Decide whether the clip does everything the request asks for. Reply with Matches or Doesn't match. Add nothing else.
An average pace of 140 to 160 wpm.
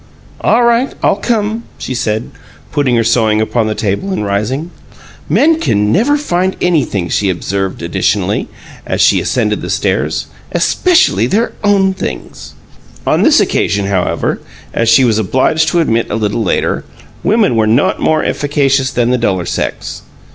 Matches